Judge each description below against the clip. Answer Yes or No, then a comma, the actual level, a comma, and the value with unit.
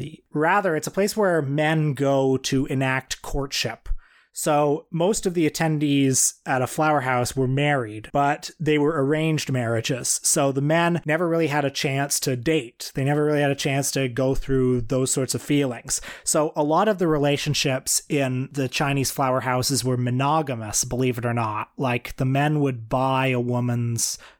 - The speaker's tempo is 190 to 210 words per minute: No, average, 180 wpm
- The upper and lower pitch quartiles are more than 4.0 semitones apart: No, average, 2.9 semitones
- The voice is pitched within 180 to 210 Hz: No, medium, 140 Hz